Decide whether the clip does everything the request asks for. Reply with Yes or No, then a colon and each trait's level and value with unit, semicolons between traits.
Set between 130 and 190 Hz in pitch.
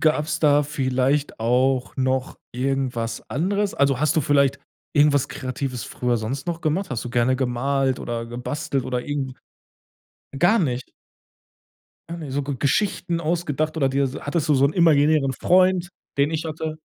Yes: medium, 140 Hz